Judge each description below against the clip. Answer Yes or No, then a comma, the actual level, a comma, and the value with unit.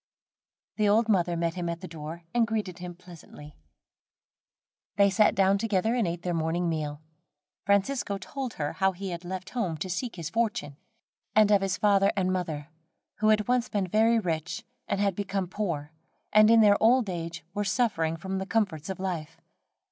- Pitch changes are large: No, average, 3.9 semitones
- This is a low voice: No, high, 190 Hz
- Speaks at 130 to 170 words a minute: No, average, 185 wpm